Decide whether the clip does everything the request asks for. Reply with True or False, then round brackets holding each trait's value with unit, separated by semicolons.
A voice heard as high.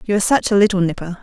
True (195 Hz)